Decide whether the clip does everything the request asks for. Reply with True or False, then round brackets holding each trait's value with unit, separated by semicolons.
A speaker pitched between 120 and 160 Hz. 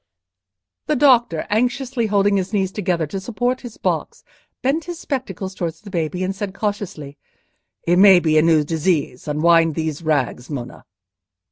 False (190 Hz)